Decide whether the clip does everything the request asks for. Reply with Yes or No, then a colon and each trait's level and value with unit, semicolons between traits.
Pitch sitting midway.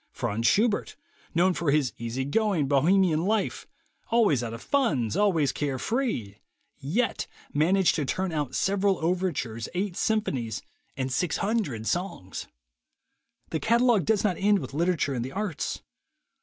Yes: medium, 170 Hz